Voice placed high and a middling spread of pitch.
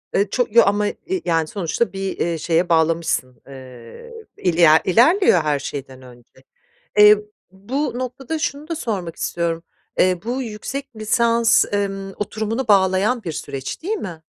No: high, 195 Hz; wide, 6.2 semitones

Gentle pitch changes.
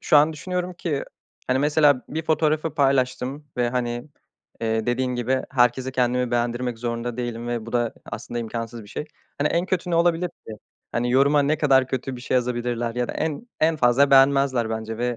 No: average, 3.5 semitones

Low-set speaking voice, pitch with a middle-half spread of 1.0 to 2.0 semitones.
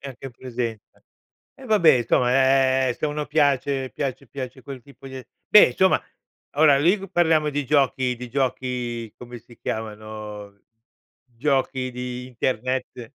No: low, 130 Hz; narrow, 2.5 semitones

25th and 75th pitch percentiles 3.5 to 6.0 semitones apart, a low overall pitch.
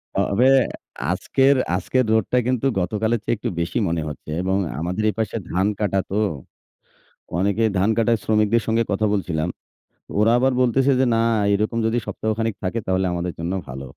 Yes: average, 3.8 semitones; low, 105 Hz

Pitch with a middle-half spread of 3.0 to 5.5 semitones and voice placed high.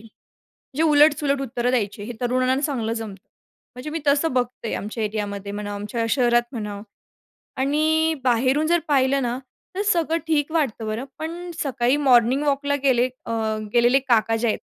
Yes: average, 4.2 semitones; very high, 255 Hz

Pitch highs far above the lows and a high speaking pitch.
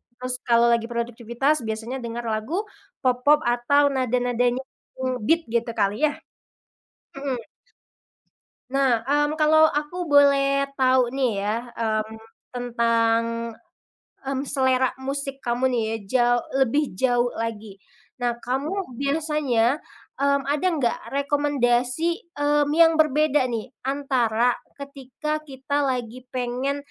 No: average, 3.2 semitones; very high, 260 Hz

